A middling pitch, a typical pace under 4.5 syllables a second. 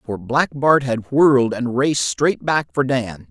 No: low, 125 Hz; 4.2 syllables/s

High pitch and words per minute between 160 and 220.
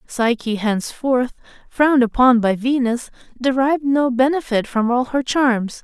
No: very high, 250 Hz; slow, 135 wpm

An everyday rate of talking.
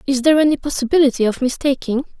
Yes: average, 165 wpm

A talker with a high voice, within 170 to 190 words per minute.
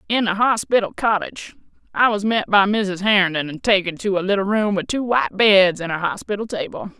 No: high, 200 Hz; fast, 205 wpm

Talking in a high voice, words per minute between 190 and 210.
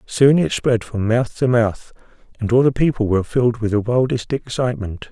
No: low, 120 Hz; average, 200 wpm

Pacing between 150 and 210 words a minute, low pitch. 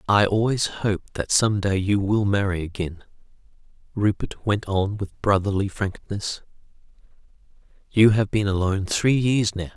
No: average, 140 wpm; low, 100 Hz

